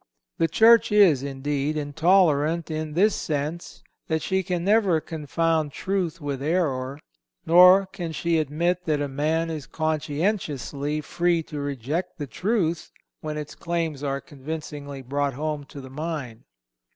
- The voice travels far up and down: No, average, 3.0 semitones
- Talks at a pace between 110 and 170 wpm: Yes, average, 140 wpm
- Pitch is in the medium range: Yes, medium, 155 Hz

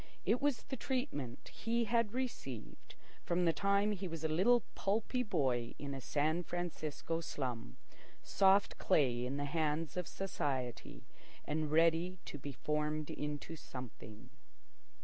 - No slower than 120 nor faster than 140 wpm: Yes, slow, 135 wpm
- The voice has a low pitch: No, medium, 160 Hz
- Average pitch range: No, wide, 5.8 semitones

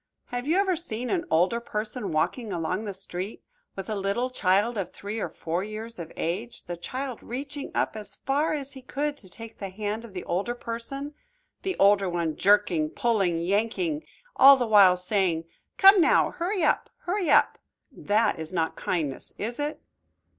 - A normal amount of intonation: No, wide, 6.2 semitones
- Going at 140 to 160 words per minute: No, average, 180 wpm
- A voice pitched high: Yes, high, 215 Hz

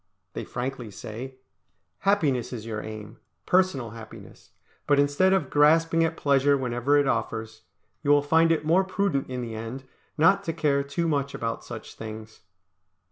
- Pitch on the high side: No, medium, 140 Hz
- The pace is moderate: Yes, average, 160 wpm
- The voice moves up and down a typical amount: No, wide, 5.9 semitones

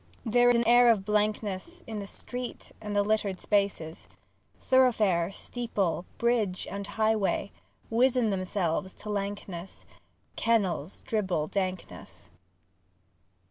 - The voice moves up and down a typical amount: Yes, average, 3.3 semitones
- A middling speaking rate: No, slow, 115 wpm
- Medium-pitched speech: No, high, 205 Hz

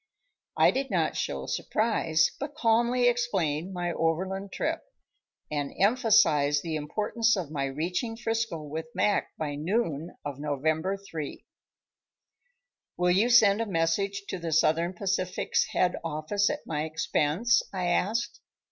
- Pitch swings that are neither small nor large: No, wide, 6.0 semitones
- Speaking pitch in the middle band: Yes, medium, 180 Hz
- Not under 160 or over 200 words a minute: No, slow, 135 wpm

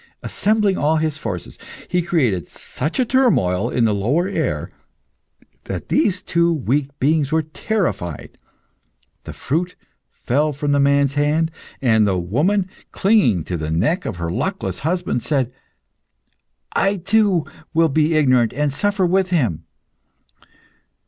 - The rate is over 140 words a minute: No, slow, 135 wpm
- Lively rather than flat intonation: Yes, wide, 6.9 semitones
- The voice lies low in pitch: No, medium, 150 Hz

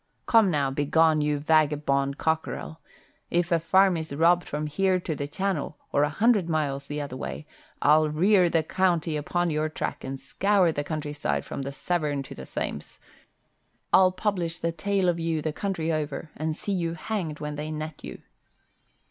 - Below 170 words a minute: No, average, 180 wpm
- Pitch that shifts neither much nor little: Yes, average, 3.0 semitones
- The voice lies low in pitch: No, medium, 155 Hz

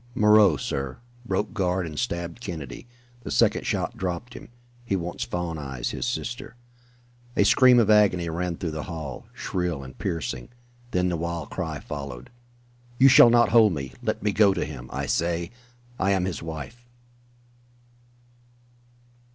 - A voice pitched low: Yes, very low, 90 Hz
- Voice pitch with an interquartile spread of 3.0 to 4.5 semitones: No, average, 4.9 semitones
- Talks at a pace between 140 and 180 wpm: Yes, average, 155 wpm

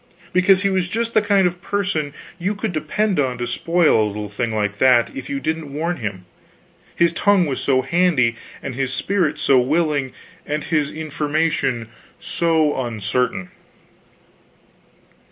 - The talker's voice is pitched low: No, medium, 150 Hz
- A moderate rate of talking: Yes, average, 155 wpm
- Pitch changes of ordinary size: No, wide, 5.9 semitones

